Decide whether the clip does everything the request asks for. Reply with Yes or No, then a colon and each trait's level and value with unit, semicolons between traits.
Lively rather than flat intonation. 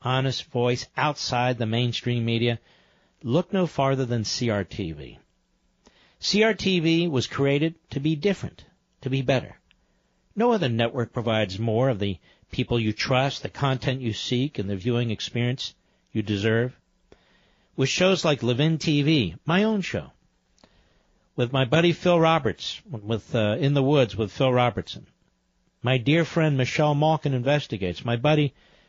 No: average, 4.6 semitones